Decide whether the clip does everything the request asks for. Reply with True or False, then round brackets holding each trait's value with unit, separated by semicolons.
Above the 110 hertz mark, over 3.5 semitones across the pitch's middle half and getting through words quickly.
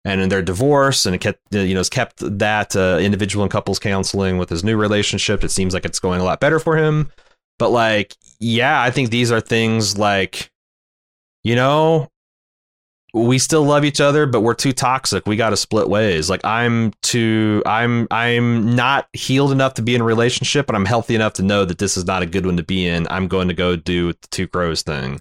False (105 Hz; 4.3 semitones; 225 wpm)